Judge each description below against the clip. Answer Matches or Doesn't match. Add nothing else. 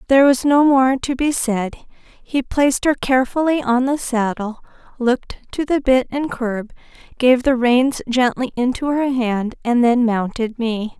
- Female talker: Matches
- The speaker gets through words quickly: Doesn't match